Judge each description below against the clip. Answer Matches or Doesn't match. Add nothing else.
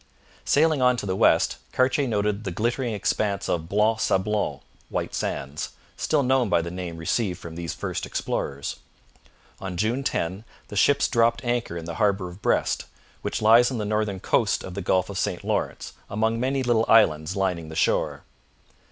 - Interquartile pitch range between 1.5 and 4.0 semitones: Doesn't match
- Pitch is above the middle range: Doesn't match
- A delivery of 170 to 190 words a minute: Matches